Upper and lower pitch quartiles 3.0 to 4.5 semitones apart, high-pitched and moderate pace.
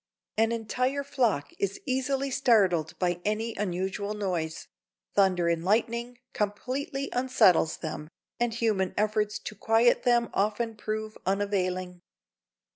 No: average, 4.2 semitones; high, 210 Hz; slow, 120 wpm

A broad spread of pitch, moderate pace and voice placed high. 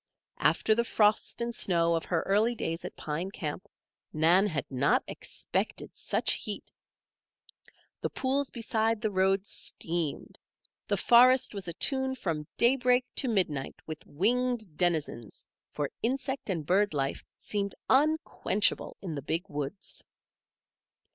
No: wide, 6.6 semitones; slow, 130 wpm; high, 195 Hz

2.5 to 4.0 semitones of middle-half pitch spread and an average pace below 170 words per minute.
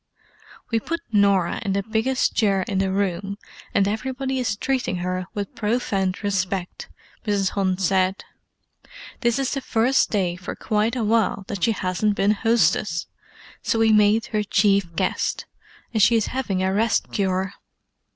Yes: average, 2.8 semitones; average, 160 wpm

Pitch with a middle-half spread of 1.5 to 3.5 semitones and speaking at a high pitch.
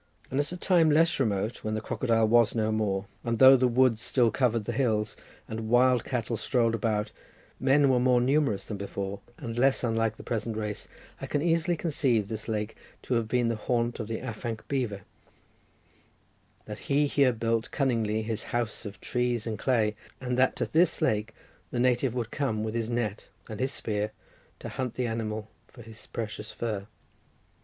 No: average, 2.8 semitones; low, 115 Hz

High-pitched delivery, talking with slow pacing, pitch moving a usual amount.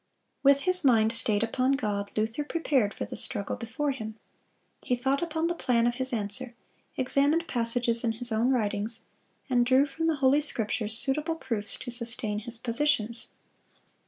No: high, 245 Hz; average, 165 wpm; average, 3.7 semitones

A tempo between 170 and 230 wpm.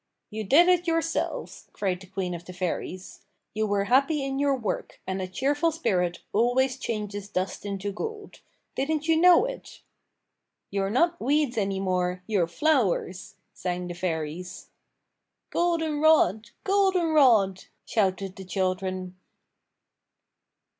No: slow, 135 wpm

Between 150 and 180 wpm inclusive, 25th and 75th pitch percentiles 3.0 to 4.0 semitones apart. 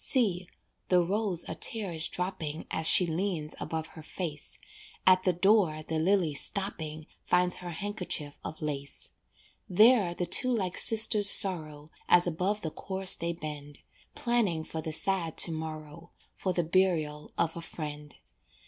Yes: average, 155 wpm; average, 3.5 semitones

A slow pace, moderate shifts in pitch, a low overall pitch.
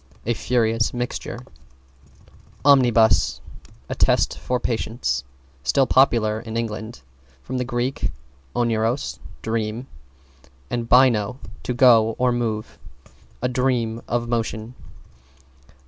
No: slow, 100 wpm; narrow, 1.9 semitones; low, 115 Hz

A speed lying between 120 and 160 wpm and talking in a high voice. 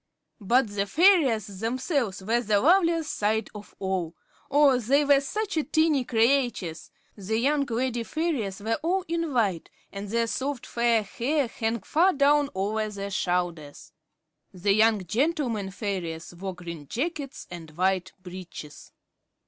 Yes: average, 140 wpm; high, 225 Hz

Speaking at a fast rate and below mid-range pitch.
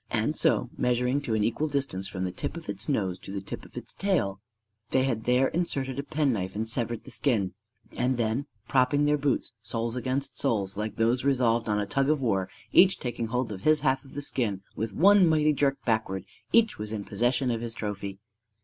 Yes: fast, 215 wpm; low, 120 Hz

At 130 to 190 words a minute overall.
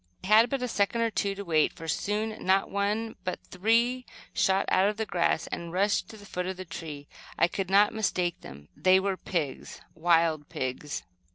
No: average, 200 wpm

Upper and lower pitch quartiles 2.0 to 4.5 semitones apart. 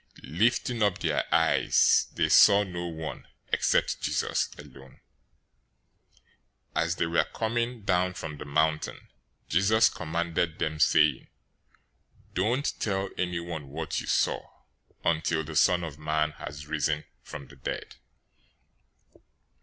Yes: average, 3.7 semitones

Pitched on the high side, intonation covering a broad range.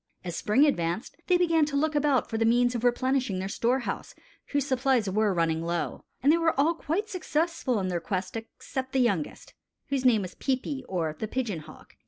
Yes: high, 245 Hz; wide, 6.8 semitones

